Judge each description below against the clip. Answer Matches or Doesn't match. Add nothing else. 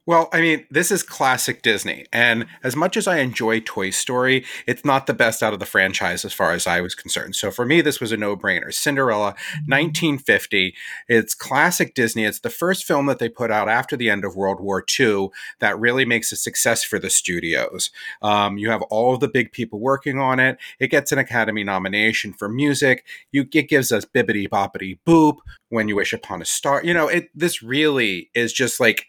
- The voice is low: Matches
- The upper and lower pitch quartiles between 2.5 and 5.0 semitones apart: Doesn't match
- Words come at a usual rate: Doesn't match